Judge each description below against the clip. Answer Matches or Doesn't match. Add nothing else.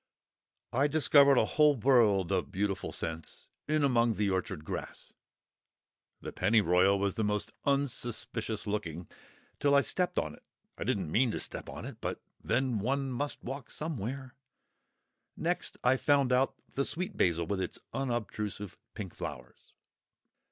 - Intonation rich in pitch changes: Matches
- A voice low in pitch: Matches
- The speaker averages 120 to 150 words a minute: Matches